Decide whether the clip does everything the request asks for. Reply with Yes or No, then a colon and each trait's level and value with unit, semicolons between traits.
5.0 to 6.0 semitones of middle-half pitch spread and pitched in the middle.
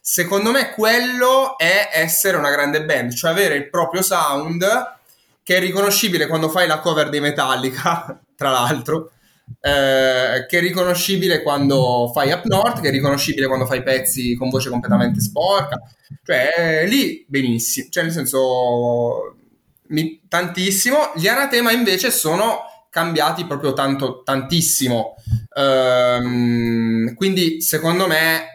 Yes: wide, 5.5 semitones; medium, 155 Hz